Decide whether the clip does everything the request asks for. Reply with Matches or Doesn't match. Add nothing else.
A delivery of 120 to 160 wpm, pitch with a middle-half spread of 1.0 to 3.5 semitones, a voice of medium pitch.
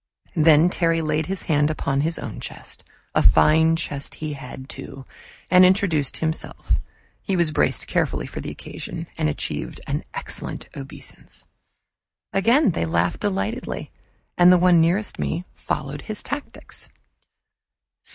Doesn't match